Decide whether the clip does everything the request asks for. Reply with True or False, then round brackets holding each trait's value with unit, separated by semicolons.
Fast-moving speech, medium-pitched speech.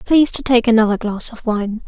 False (225 wpm; 230 Hz)